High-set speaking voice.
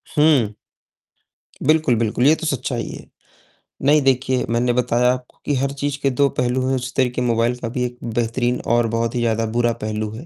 No: low, 125 Hz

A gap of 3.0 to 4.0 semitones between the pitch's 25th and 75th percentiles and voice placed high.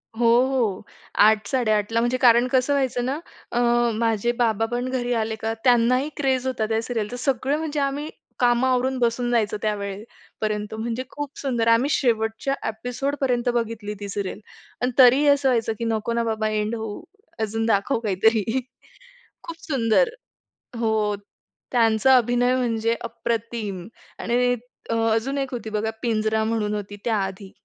No: narrow, 2.6 semitones; high, 235 Hz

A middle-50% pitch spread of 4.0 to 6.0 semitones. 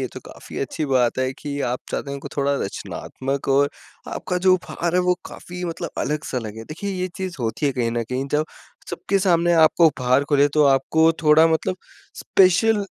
Yes: average, 4.6 semitones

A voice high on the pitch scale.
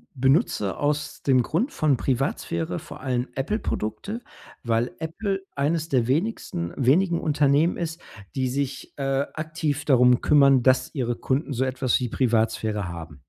No: low, 135 Hz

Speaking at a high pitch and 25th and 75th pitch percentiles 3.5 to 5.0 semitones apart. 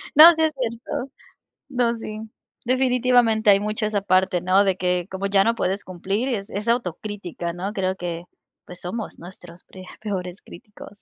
Yes: high, 205 Hz; average, 4.1 semitones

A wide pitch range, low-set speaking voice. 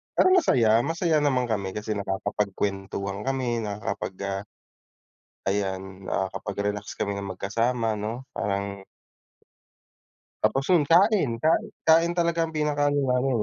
Yes: wide, 6.5 semitones; low, 110 Hz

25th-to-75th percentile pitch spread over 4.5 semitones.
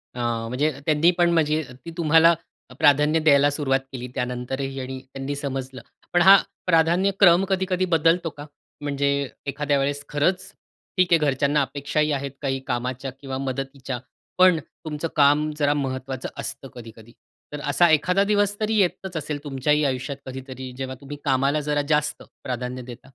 No: average, 3.4 semitones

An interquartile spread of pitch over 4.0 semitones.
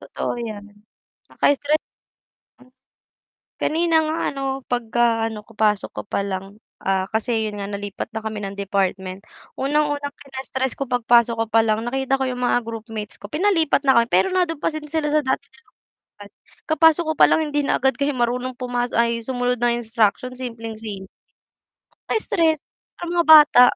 Yes: average, 4.4 semitones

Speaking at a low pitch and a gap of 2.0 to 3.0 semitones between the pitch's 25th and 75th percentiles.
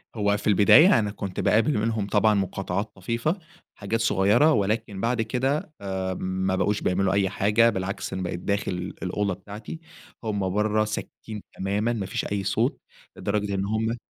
Yes: low, 105 Hz; narrow, 2.5 semitones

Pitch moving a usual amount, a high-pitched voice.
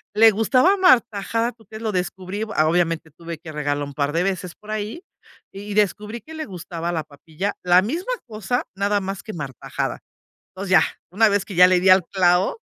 Yes: average, 4.0 semitones; high, 195 Hz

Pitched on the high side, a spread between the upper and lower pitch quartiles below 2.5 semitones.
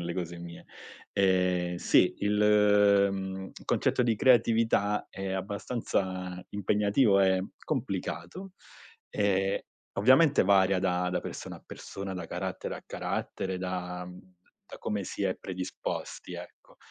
No: very low, 95 Hz; narrow, 2.1 semitones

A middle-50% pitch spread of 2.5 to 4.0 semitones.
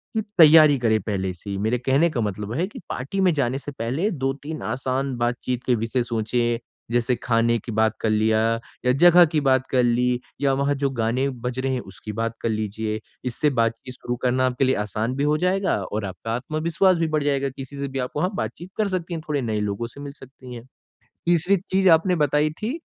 No: average, 4.5 semitones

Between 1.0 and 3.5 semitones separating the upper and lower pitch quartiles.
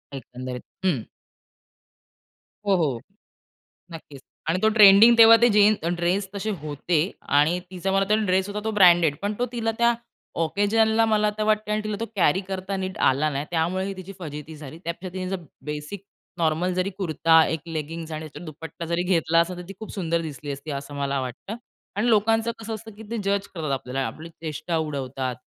No: average, 4.9 semitones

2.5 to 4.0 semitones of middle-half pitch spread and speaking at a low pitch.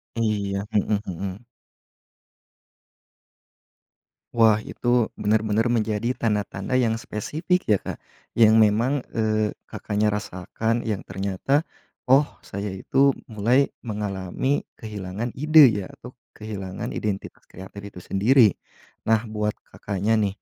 Yes: average, 2.8 semitones; low, 110 Hz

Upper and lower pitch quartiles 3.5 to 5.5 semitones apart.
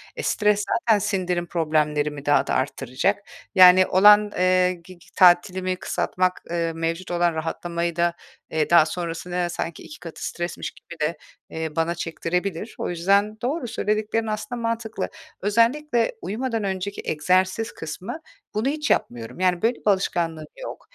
Yes: average, 3.9 semitones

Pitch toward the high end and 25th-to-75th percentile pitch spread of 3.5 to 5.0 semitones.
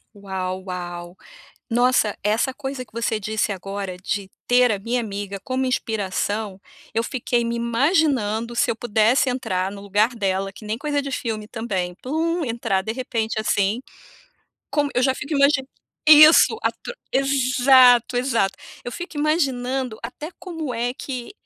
Yes: high, 235 Hz; average, 4.5 semitones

